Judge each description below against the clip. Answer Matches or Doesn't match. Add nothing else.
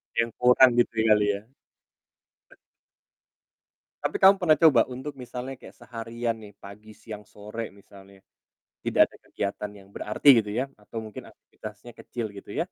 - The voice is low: Matches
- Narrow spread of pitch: Doesn't match